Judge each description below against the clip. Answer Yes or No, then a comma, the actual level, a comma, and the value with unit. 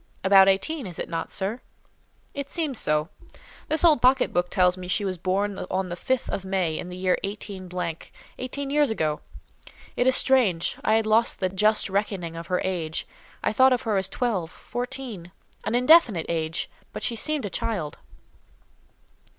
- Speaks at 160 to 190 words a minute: Yes, average, 170 wpm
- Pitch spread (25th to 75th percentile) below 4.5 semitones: No, wide, 5.5 semitones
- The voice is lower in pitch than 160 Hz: No, high, 195 Hz